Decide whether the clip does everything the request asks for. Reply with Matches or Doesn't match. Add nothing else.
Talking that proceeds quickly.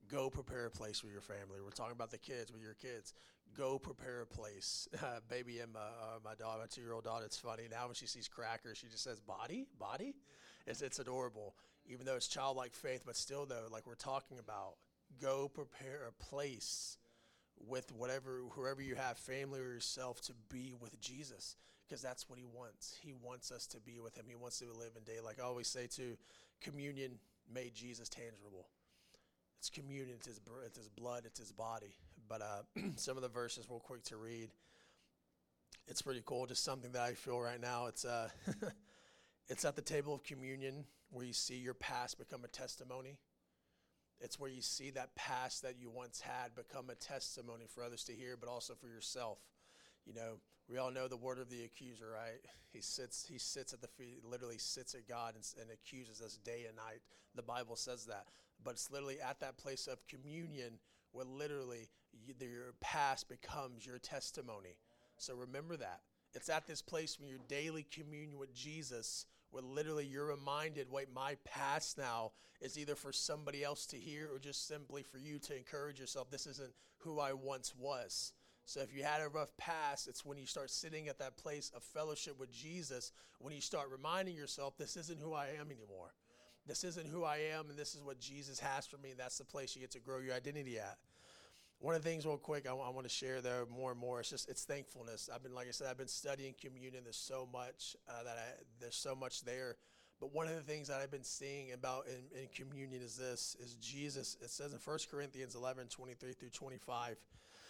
Matches